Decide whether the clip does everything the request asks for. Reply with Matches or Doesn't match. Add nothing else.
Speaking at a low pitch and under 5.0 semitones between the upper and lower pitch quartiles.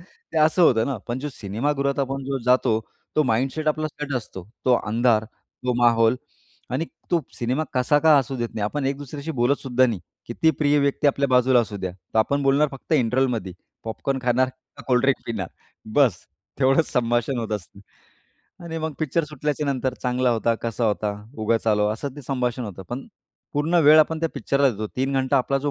Matches